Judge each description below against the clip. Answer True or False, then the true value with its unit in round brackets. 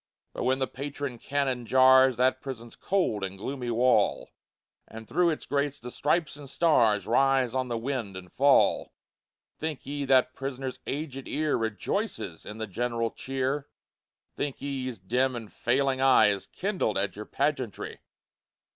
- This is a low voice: True (130 Hz)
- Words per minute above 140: True (155 wpm)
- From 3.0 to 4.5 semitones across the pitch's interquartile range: True (3.4 semitones)